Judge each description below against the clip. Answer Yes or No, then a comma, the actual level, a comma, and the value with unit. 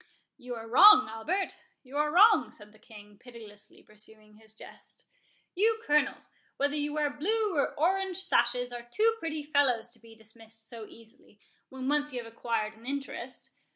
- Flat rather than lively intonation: No, average, 5.2 semitones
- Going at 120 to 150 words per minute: No, average, 170 wpm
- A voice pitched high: Yes, very high, 250 Hz